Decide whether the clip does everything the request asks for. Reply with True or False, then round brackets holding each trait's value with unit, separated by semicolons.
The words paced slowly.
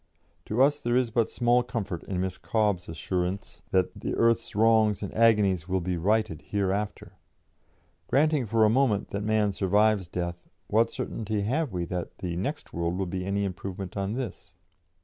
False (170 wpm)